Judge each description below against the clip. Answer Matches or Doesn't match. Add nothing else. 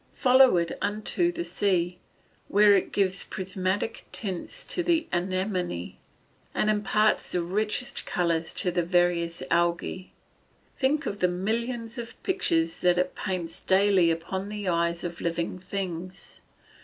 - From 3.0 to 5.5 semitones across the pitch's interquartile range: Matches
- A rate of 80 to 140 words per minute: Matches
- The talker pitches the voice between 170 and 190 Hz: Matches